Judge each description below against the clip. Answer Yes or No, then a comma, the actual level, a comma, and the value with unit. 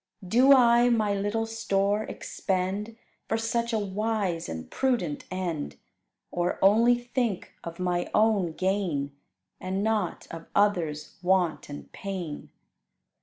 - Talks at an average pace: No, slow, 120 wpm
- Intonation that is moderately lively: Yes, average, 4.1 semitones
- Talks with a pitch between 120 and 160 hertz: No, high, 200 Hz